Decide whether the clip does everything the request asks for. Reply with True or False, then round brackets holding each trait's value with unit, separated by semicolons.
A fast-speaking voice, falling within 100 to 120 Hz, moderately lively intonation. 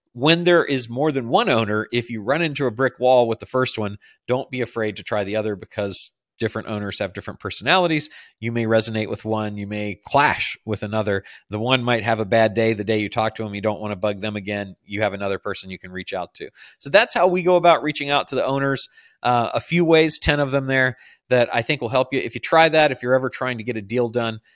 True (265 wpm; 115 Hz; 3.8 semitones)